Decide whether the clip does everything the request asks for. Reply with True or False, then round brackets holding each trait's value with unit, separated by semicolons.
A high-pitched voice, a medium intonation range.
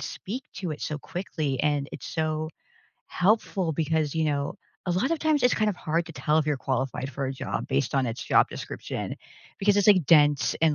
False (155 Hz; 4.6 semitones)